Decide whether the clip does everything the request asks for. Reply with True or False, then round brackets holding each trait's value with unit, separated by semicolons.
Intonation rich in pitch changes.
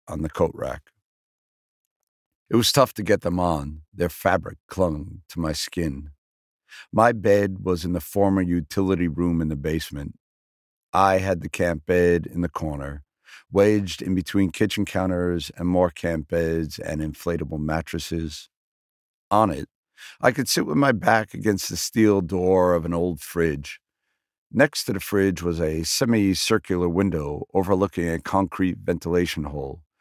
False (3.1 semitones)